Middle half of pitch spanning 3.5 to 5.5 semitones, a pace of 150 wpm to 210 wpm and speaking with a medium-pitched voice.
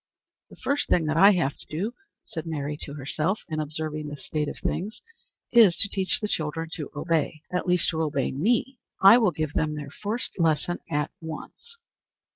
Yes: average, 4.1 semitones; average, 190 wpm; medium, 160 Hz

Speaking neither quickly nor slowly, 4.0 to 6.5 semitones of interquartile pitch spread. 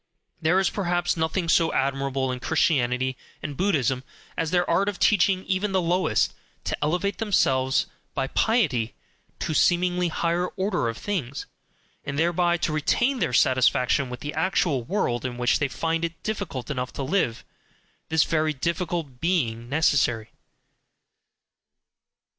Yes: average, 145 wpm; wide, 5.4 semitones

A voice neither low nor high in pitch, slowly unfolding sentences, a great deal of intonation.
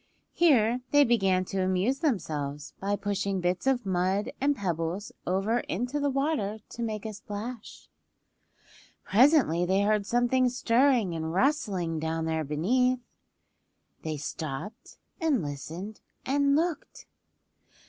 No: high, 205 Hz; slow, 125 wpm; wide, 6.2 semitones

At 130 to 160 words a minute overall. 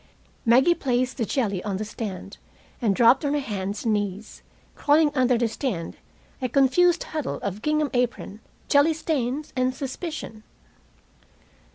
Yes: average, 145 wpm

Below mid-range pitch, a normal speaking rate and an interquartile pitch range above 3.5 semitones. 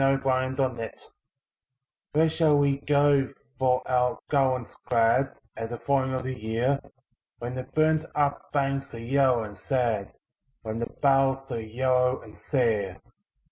No: low, 130 Hz; average, 150 wpm; average, 2.7 semitones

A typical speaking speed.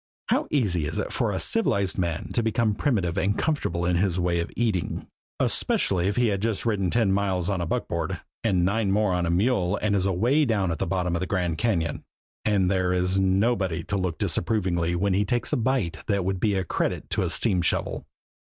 No: fast, 220 wpm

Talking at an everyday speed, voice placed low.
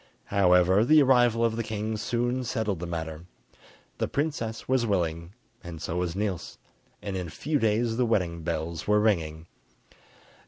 Yes: average, 160 wpm; low, 105 Hz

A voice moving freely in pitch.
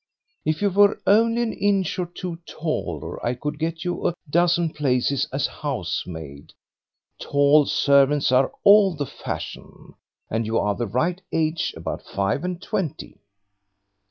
Yes: wide, 5.8 semitones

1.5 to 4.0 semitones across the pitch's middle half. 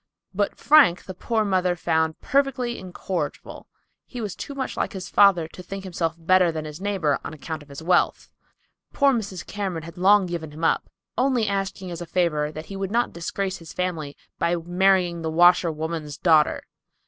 Yes: average, 3.4 semitones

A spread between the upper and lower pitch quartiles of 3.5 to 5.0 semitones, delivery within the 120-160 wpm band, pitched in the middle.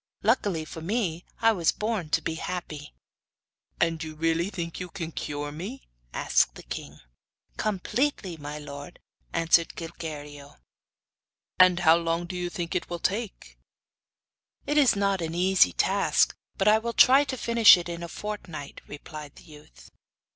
Yes: average, 4.0 semitones; average, 155 wpm; medium, 170 Hz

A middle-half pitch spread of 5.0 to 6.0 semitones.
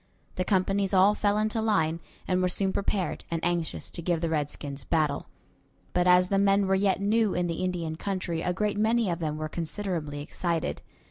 No: average, 3.4 semitones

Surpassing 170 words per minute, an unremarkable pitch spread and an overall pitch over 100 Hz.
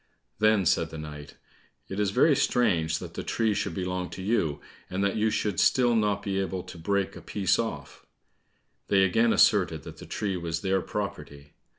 No: average, 190 wpm; average, 4.1 semitones; very low, 95 Hz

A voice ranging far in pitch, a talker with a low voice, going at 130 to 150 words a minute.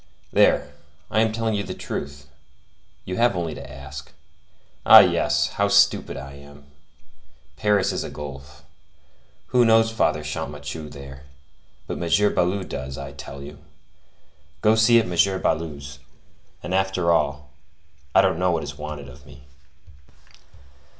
Yes: wide, 6.2 semitones; very low, 80 Hz; average, 140 wpm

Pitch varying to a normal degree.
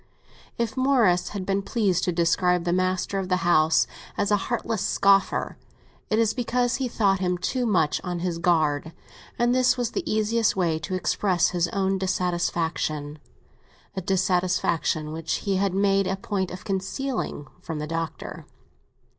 Yes: average, 3.3 semitones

